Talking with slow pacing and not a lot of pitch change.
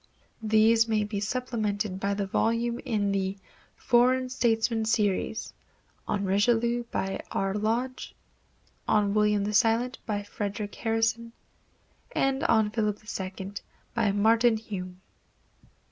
Yes: slow, 115 wpm; narrow, 2.3 semitones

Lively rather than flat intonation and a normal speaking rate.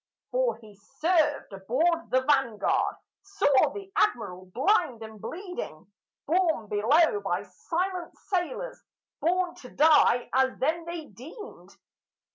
No: wide, 7.2 semitones; slow, 115 wpm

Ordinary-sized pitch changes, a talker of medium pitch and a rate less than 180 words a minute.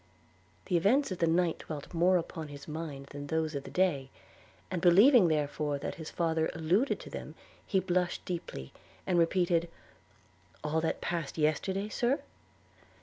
Yes: average, 3.0 semitones; medium, 165 Hz; average, 155 wpm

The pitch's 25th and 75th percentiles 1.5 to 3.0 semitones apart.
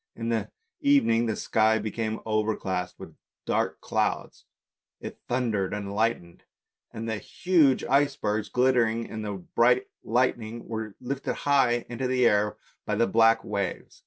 Yes: average, 2.7 semitones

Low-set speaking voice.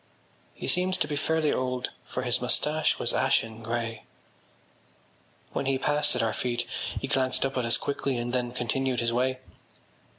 Yes: low, 125 Hz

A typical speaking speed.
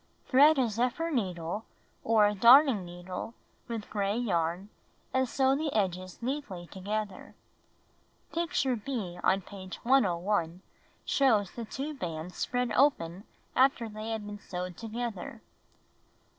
No: slow, 125 wpm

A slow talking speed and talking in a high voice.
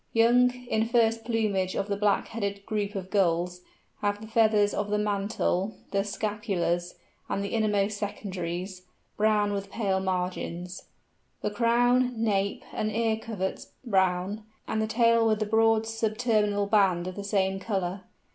No: average, 155 wpm; high, 205 Hz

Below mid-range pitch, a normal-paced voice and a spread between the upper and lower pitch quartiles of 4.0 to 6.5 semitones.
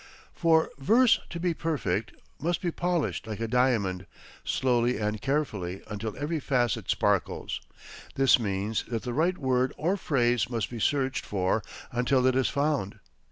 Yes: low, 125 Hz; average, 155 wpm; wide, 5.5 semitones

